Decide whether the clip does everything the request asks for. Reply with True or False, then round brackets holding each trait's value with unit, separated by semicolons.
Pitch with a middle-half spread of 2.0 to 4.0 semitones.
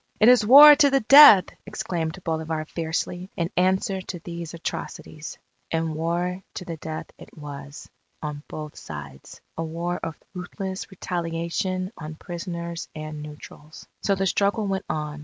True (3.2 semitones)